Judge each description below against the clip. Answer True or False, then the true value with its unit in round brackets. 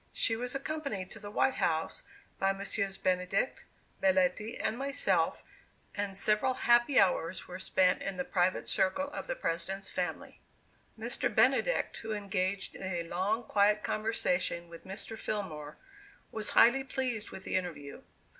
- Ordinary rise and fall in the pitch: True (3.6 semitones)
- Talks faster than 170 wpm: False (145 wpm)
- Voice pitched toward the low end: False (195 Hz)